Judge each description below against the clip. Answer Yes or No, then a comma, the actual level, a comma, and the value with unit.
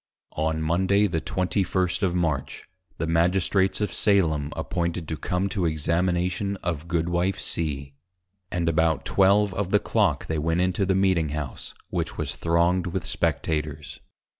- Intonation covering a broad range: No, average, 2.9 semitones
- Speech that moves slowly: No, average, 145 wpm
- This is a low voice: Yes, very low, 85 Hz